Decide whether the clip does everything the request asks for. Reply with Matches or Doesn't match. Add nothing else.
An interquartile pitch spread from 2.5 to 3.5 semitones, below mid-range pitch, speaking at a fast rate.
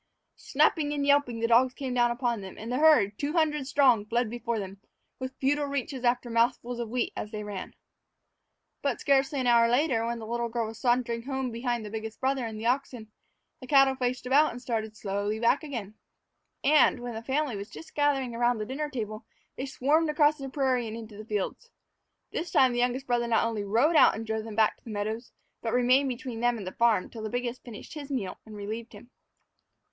Doesn't match